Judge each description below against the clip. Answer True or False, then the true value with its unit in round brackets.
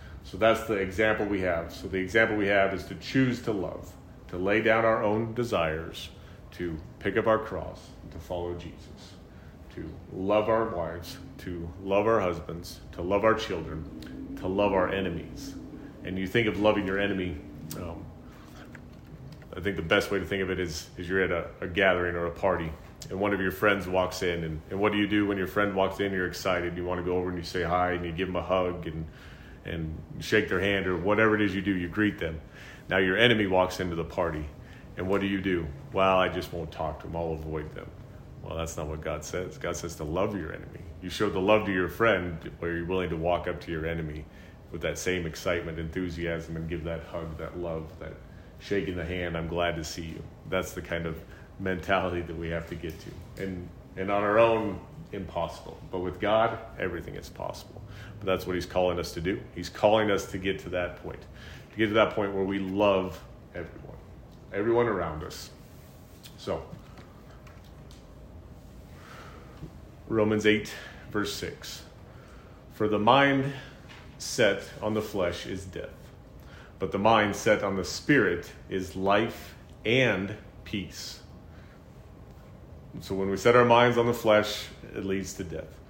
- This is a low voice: True (95 Hz)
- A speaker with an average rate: True (195 wpm)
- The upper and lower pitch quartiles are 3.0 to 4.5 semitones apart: True (3.3 semitones)